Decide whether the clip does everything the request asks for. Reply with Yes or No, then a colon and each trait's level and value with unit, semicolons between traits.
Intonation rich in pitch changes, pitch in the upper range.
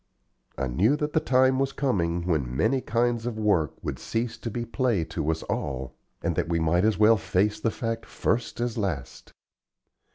No: wide, 6.4 semitones; low, 110 Hz